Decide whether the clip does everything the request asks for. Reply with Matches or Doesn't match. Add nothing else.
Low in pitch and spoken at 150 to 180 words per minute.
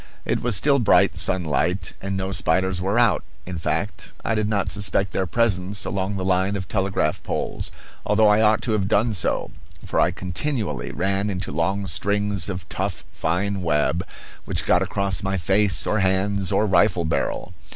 Matches